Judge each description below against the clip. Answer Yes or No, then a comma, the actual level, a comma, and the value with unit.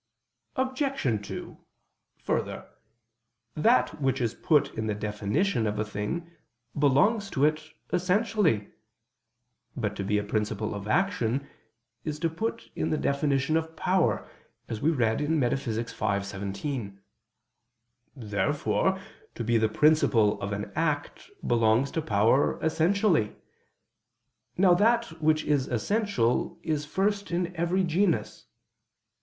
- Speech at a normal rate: No, slow, 125 wpm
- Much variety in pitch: Yes, wide, 7.7 semitones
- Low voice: No, medium, 145 Hz